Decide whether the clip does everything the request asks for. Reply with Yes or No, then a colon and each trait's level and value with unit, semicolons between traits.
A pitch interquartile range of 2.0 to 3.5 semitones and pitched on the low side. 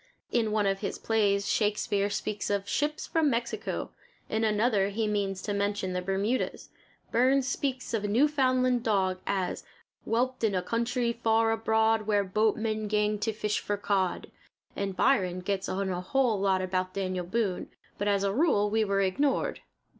No: average, 2.8 semitones; high, 210 Hz